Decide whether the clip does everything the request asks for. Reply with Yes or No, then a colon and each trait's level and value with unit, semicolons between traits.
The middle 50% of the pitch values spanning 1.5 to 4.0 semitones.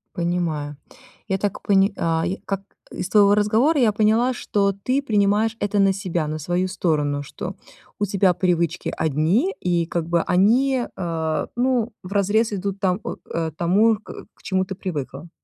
Yes: average, 3.7 semitones